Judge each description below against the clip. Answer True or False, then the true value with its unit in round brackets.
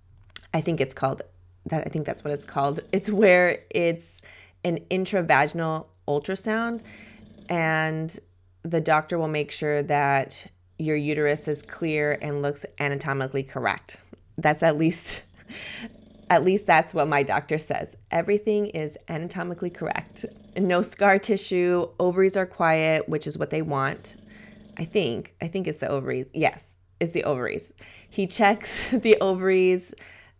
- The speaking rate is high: False (140 wpm)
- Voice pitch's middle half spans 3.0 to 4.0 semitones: False (4.9 semitones)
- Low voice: False (160 Hz)